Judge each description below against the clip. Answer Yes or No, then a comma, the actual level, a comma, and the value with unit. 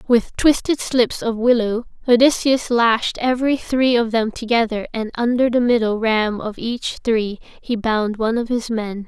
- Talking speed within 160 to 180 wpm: Yes, average, 170 wpm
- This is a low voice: No, high, 230 Hz